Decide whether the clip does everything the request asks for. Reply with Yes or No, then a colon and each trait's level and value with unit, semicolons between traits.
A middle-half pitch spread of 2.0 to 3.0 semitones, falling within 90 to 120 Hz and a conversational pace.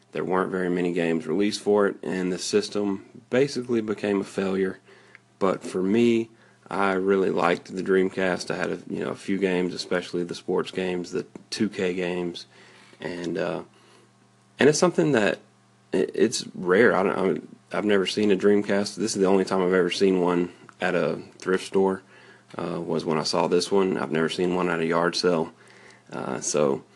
Yes: narrow, 2.4 semitones; very low, 95 Hz; average, 185 wpm